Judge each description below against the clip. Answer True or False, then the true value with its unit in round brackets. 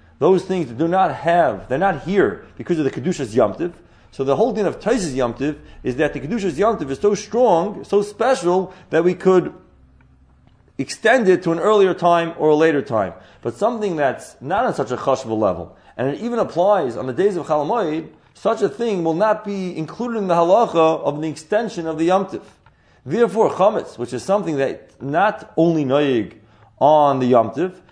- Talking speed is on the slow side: False (190 wpm)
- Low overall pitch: False (170 Hz)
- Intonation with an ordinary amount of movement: False (5.8 semitones)